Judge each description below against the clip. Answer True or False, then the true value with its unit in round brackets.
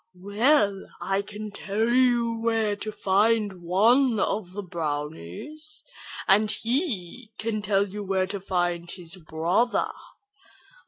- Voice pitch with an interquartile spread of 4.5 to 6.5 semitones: False (3.6 semitones)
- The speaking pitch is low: False (205 Hz)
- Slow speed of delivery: True (120 wpm)